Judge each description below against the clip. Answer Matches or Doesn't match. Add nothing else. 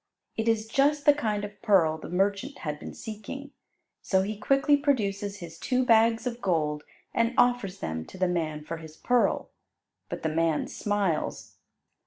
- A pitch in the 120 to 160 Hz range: Doesn't match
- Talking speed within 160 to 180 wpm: Matches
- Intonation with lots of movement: Matches